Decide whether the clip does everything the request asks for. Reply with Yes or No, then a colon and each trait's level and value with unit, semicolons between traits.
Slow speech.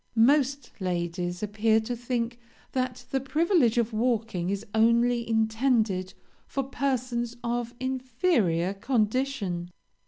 Yes: slow, 105 wpm